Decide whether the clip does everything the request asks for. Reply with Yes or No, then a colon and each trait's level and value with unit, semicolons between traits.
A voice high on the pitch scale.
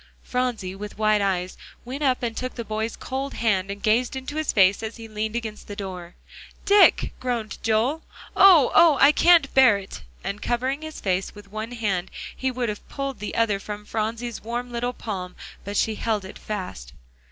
Yes: high, 225 Hz